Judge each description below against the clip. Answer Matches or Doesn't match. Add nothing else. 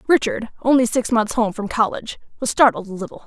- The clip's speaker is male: Doesn't match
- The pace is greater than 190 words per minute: Matches